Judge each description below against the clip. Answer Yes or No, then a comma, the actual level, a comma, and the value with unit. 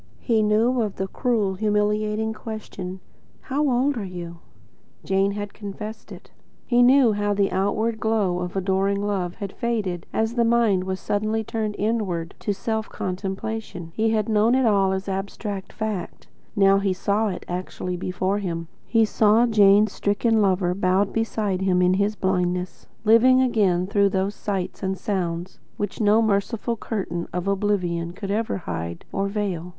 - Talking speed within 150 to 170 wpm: Yes, average, 165 wpm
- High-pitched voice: Yes, high, 200 Hz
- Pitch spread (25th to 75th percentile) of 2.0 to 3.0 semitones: Yes, average, 2.7 semitones